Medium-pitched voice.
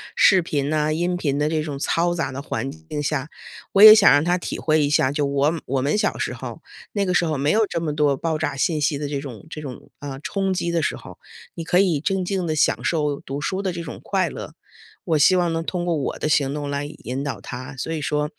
Yes: medium, 155 Hz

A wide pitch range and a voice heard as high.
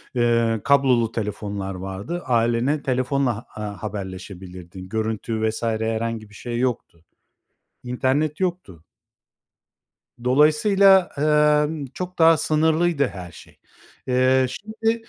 No: wide, 6.1 semitones; low, 120 Hz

